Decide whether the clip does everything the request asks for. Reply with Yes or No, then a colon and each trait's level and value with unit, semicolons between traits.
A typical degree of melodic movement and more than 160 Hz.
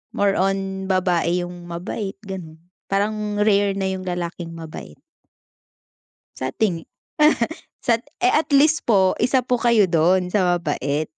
Yes: average, 3.2 semitones; high, 190 Hz